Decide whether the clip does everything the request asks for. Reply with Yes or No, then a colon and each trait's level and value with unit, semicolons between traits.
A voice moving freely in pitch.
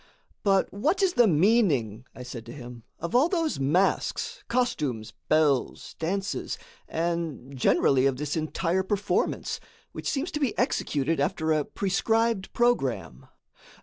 Yes: wide, 8.7 semitones